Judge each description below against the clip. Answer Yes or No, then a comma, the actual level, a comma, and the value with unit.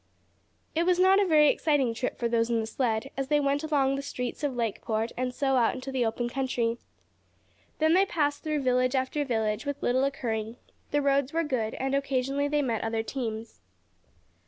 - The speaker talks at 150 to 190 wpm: No, average, 200 wpm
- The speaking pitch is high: Yes, very high, 265 Hz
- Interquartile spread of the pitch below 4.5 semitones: Yes, average, 3.6 semitones